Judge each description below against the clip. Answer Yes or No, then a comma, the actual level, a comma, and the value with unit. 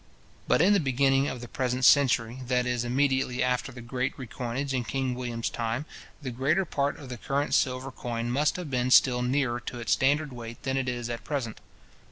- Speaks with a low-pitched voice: Yes, low, 130 Hz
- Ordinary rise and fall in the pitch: No, narrow, 2.1 semitones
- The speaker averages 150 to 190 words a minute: No, fast, 205 wpm